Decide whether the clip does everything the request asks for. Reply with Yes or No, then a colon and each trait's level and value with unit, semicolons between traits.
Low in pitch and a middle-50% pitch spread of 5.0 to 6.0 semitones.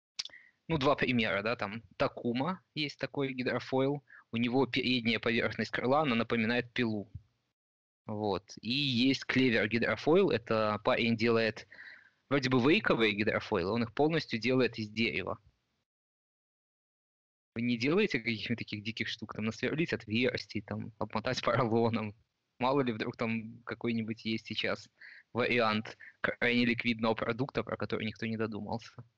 No: low, 115 Hz; narrow, 2.4 semitones